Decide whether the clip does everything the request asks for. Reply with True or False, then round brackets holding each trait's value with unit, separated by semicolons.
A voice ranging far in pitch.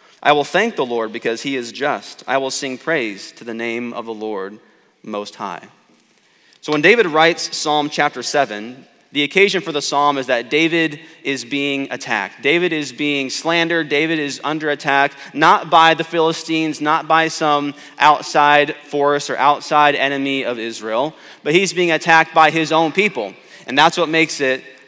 False (3.0 semitones)